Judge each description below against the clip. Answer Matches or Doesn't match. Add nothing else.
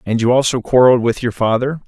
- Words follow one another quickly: Matches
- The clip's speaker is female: Doesn't match